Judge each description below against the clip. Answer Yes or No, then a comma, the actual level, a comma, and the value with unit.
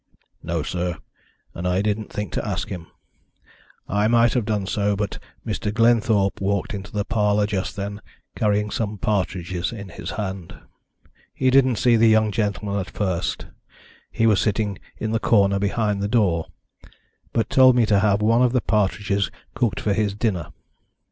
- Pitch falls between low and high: No, low, 105 Hz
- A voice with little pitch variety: Yes, narrow, 2.0 semitones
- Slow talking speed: No, average, 170 wpm